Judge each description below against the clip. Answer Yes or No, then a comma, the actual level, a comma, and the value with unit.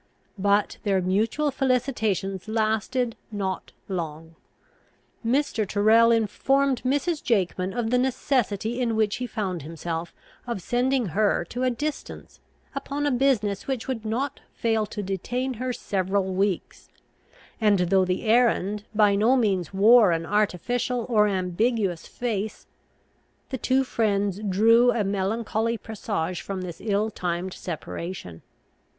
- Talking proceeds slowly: Yes, slow, 130 wpm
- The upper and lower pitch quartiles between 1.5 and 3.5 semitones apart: No, average, 4.2 semitones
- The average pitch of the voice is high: Yes, high, 215 Hz